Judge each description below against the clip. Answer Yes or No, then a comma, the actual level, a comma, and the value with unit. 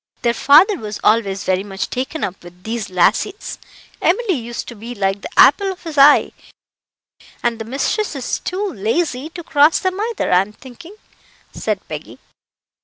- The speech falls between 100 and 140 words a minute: No, average, 165 wpm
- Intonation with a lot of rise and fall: Yes, wide, 8.5 semitones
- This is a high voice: Yes, very high, 250 Hz